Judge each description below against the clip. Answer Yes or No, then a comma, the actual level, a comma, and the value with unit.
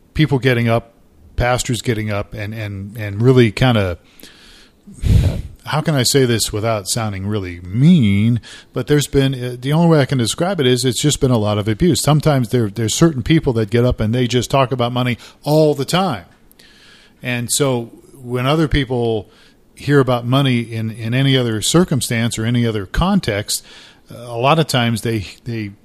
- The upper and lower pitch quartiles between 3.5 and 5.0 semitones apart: Yes, average, 3.8 semitones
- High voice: No, low, 125 Hz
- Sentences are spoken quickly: No, average, 185 wpm